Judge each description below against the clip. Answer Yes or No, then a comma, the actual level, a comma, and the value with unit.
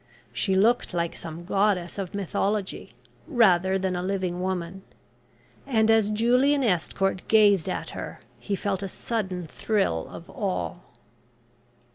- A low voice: No, high, 195 Hz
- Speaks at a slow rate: Yes, slow, 130 wpm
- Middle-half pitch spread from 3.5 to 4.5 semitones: No, average, 2.9 semitones